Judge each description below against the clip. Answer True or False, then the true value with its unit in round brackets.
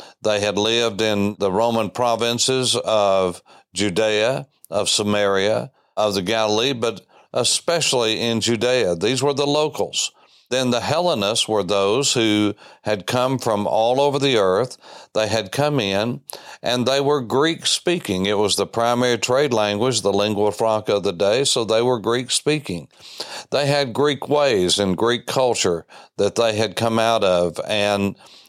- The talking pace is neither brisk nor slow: True (160 wpm)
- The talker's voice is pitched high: False (115 Hz)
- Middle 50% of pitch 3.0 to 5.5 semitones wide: True (3.5 semitones)